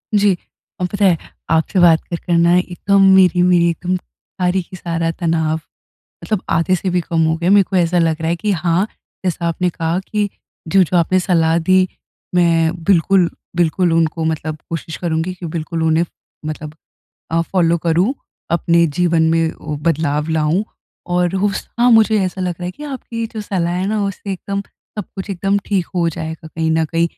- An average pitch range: No, narrow, 2.3 semitones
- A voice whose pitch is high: No, medium, 175 Hz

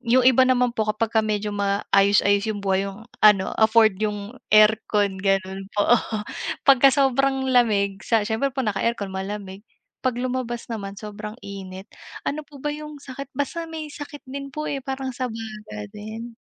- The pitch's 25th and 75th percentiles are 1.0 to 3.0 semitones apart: No, average, 4.4 semitones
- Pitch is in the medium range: No, high, 220 Hz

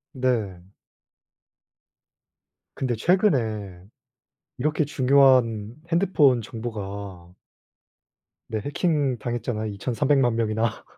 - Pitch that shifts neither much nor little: Yes, average, 4.3 semitones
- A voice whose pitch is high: No, low, 120 Hz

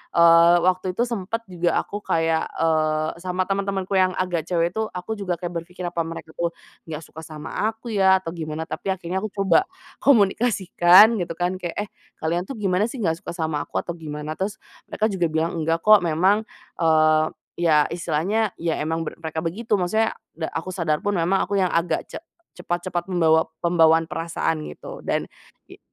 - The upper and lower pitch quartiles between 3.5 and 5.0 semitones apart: No, average, 2.9 semitones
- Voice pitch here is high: No, medium, 175 Hz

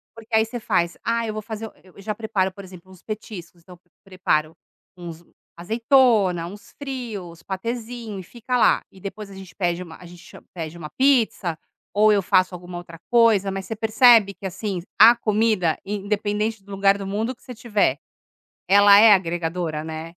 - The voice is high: Yes, high, 200 Hz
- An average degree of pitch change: Yes, average, 3.8 semitones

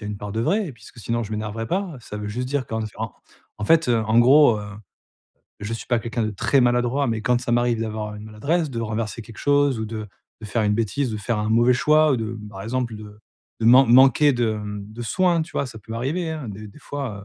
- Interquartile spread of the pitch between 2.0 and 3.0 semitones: No, average, 3.7 semitones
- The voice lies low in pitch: Yes, low, 115 Hz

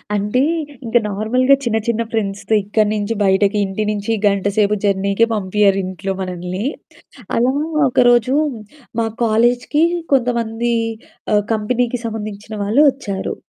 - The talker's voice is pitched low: No, high, 215 Hz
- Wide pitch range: No, average, 3.1 semitones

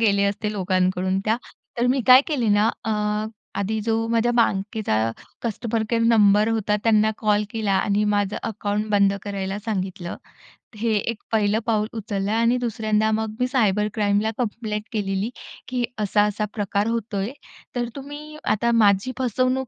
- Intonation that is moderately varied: No, narrow, 2.2 semitones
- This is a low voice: No, high, 215 Hz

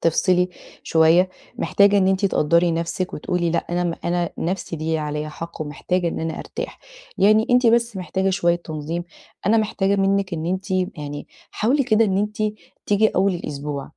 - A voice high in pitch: No, medium, 180 Hz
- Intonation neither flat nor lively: Yes, average, 3.3 semitones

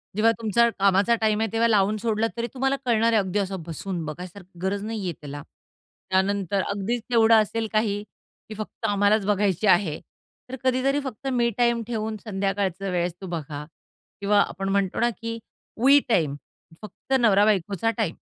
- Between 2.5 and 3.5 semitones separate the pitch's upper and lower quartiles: Yes, average, 3.1 semitones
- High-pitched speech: Yes, high, 205 Hz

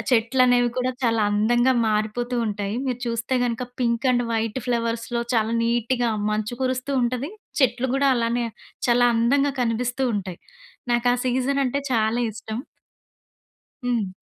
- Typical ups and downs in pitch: No, narrow, 1.7 semitones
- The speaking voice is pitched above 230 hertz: Yes, high, 240 Hz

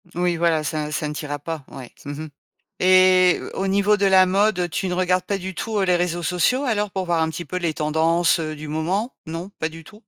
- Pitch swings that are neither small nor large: Yes, average, 3.0 semitones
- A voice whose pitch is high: No, medium, 175 Hz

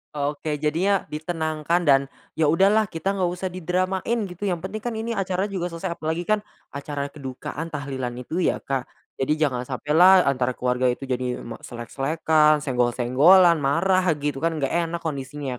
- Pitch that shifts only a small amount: No, average, 4.7 semitones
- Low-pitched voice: No, medium, 155 Hz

